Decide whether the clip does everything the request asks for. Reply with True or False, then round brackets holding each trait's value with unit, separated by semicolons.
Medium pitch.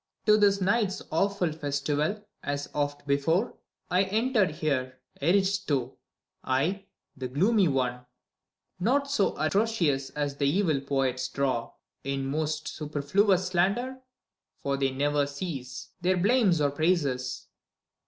True (155 Hz)